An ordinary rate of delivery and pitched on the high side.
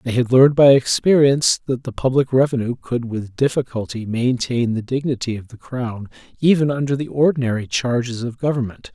No: average, 170 wpm; low, 125 Hz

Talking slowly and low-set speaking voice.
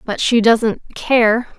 No: slow, 115 wpm; high, 230 Hz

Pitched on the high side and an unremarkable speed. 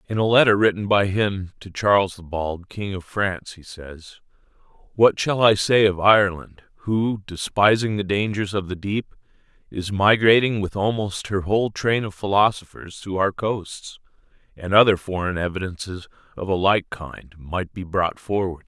No: low, 100 Hz; average, 165 wpm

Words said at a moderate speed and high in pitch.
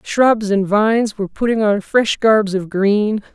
Yes: average, 180 wpm; high, 210 Hz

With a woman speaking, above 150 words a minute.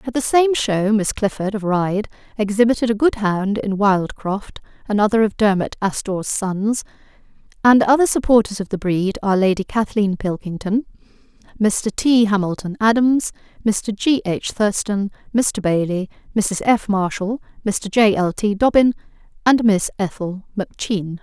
No: female; average, 145 wpm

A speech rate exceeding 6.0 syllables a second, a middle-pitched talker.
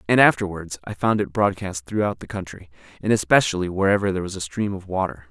No: 6.3 syllables/s; very low, 95 Hz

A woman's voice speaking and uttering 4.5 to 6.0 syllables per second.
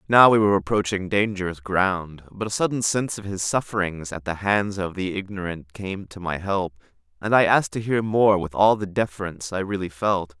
No: male; 5.3 syllables/s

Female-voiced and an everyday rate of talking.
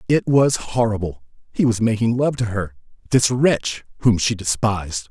No: male; average, 165 wpm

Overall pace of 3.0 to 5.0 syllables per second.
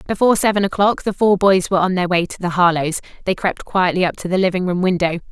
No: 6.7 syllables/s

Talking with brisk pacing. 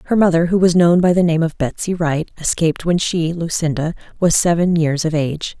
Yes: fast, 215 wpm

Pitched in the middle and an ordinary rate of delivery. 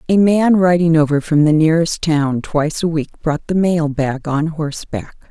Yes: medium, 160 Hz; average, 190 wpm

